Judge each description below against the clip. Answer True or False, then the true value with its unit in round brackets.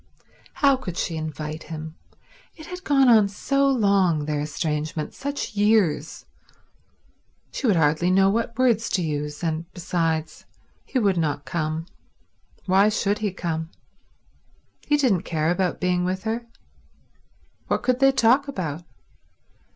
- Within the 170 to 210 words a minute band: False (135 wpm)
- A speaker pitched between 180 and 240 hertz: True (185 Hz)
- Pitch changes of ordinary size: False (6.3 semitones)